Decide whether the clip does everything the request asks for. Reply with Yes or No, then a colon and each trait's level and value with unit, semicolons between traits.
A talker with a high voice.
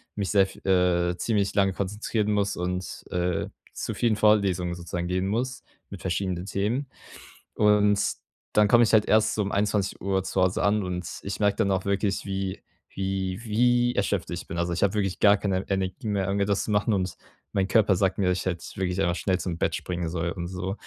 No: very low, 95 Hz